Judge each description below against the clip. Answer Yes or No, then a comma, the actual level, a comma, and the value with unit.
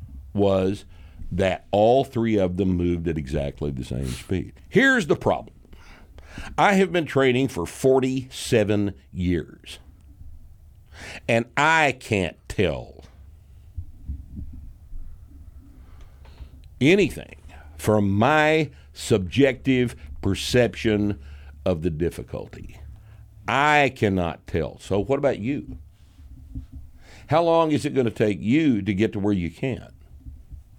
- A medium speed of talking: No, slow, 105 wpm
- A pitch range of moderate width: No, wide, 5.7 semitones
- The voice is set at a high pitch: No, very low, 90 Hz